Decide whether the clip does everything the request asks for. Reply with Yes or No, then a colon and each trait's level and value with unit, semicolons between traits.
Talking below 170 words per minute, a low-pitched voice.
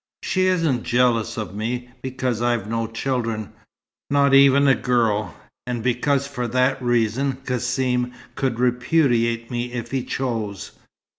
Yes: slow, 135 wpm; low, 125 Hz